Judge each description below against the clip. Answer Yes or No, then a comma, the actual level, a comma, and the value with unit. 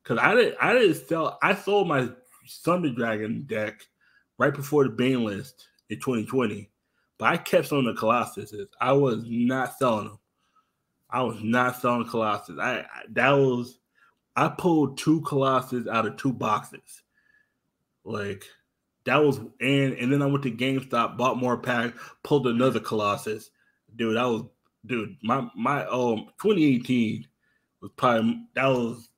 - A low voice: Yes, low, 125 Hz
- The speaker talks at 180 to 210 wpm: No, average, 155 wpm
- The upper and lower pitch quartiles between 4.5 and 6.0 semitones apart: No, average, 3.3 semitones